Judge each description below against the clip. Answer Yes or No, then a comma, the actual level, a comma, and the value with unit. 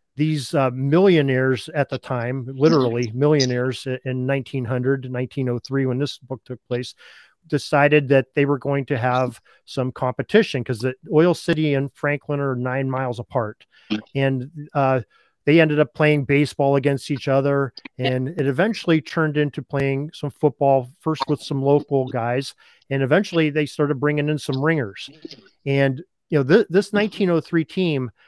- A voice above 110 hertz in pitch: Yes, medium, 140 Hz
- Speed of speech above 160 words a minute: No, average, 155 wpm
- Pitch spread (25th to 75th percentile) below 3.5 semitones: Yes, narrow, 2.6 semitones